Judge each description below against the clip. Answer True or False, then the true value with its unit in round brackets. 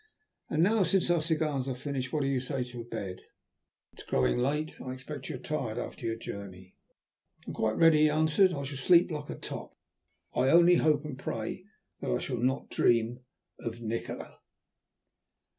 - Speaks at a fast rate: False (190 wpm)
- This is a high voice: False (135 Hz)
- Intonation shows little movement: False (4.6 semitones)